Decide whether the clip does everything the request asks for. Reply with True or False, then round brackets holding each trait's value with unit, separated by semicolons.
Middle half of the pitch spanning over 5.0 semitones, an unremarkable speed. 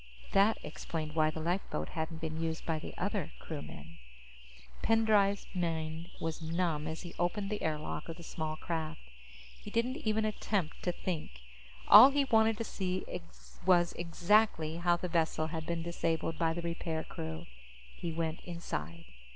False (3.3 semitones; 165 wpm)